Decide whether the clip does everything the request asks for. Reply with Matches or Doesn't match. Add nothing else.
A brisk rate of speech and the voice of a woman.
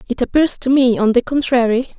Matches